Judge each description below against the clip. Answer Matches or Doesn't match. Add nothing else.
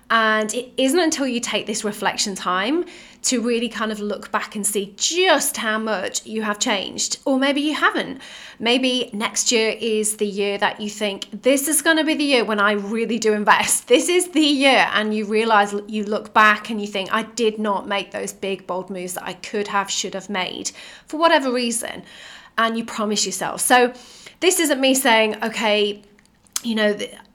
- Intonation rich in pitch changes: Doesn't match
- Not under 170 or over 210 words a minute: Matches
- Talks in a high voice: Matches